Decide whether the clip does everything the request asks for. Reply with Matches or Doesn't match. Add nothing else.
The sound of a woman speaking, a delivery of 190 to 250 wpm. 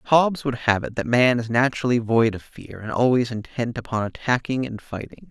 Doesn't match